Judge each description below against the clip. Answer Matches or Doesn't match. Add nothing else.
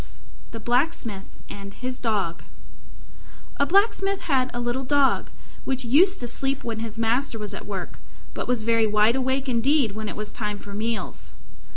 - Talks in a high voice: Matches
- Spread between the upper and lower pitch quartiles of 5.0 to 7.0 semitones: Doesn't match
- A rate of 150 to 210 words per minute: Matches